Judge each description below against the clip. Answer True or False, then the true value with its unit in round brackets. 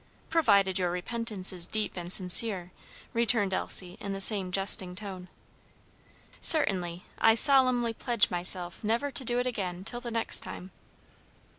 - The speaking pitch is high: True (200 Hz)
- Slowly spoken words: False (145 wpm)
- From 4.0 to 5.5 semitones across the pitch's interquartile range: True (4.3 semitones)